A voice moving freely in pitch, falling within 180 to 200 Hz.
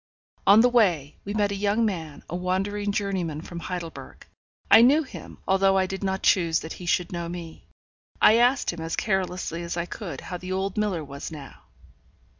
No: average, 3.2 semitones; medium, 185 Hz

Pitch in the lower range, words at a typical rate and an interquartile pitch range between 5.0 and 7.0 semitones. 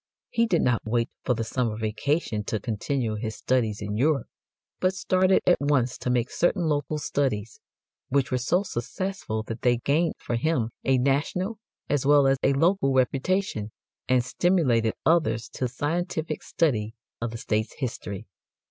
Yes: low, 130 Hz; average, 165 wpm; wide, 5.6 semitones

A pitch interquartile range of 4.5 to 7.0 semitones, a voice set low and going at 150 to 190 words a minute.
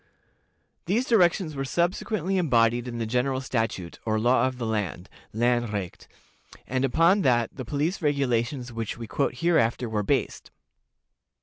No: average, 5.1 semitones; low, 125 Hz; average, 140 wpm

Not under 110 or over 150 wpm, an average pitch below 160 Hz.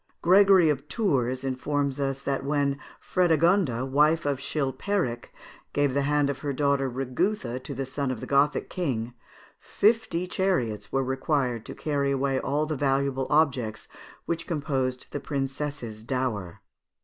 Yes: average, 145 wpm; medium, 140 Hz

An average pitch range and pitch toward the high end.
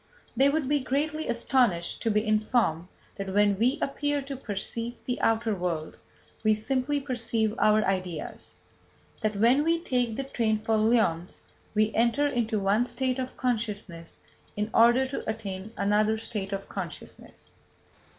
Yes: average, 3.8 semitones; high, 225 Hz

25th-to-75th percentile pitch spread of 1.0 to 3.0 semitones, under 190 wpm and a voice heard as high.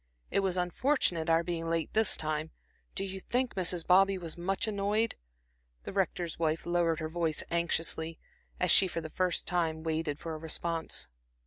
No: average, 2.7 semitones; average, 175 wpm; medium, 170 Hz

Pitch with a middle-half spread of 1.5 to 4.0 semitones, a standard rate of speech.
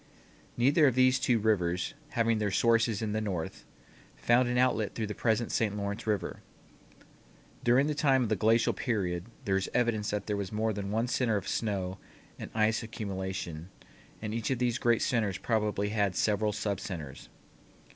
Yes: average, 2.8 semitones; average, 175 wpm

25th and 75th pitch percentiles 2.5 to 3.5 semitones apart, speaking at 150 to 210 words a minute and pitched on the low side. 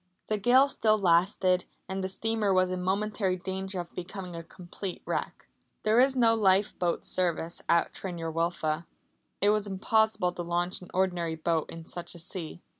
No: average, 2.9 semitones; average, 175 wpm; medium, 185 Hz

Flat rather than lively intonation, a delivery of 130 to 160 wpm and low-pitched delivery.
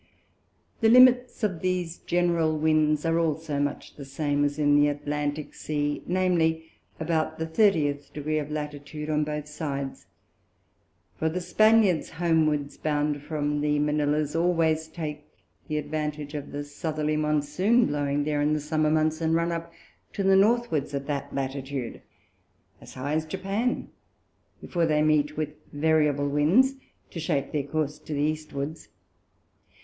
No: narrow, 2.0 semitones; average, 150 wpm; medium, 155 Hz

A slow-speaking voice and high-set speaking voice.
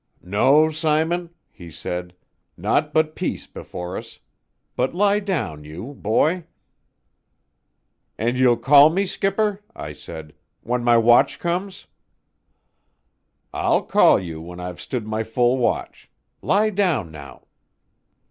No: slow, 120 wpm; low, 125 Hz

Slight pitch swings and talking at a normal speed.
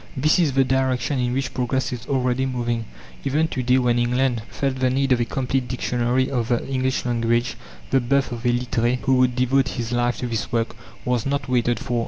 No: narrow, 1.6 semitones; fast, 215 wpm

